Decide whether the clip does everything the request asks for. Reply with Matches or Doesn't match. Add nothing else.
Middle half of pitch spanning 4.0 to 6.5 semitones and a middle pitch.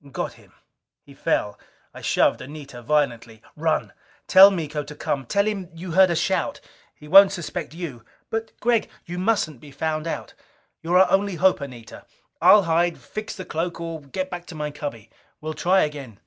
Matches